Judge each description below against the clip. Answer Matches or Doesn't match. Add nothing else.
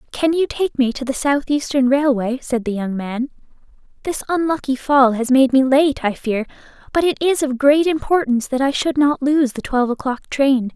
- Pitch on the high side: Matches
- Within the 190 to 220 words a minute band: Matches